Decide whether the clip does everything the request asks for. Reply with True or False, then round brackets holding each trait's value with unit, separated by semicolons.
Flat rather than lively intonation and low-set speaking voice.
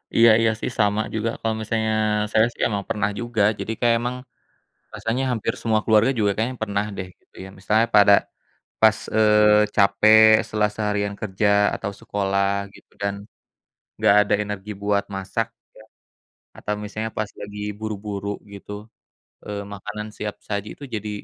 True (1.4 semitones; 105 Hz)